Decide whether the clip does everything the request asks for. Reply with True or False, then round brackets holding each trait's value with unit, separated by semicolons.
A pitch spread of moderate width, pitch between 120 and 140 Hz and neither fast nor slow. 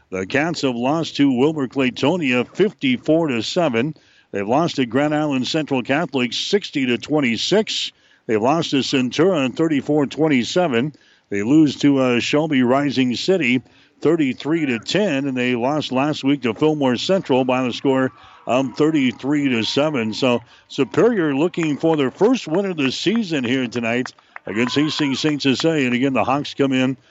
True (3.4 semitones; 135 Hz; 160 wpm)